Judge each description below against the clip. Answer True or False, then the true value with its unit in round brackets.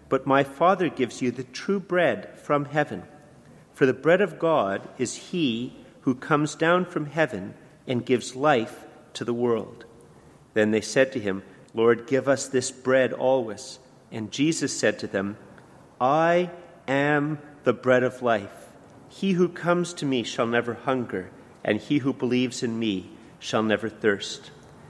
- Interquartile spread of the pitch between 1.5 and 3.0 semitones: False (4.2 semitones)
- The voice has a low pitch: True (130 Hz)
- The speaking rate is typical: True (160 wpm)